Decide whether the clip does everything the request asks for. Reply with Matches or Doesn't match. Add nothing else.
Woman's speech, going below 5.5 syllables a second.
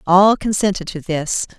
Matches